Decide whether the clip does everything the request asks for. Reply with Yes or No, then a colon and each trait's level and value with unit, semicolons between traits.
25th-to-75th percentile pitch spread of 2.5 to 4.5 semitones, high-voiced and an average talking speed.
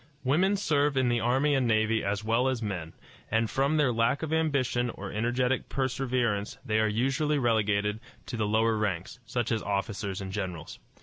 No: average, 3.9 semitones; low, 115 Hz; average, 180 wpm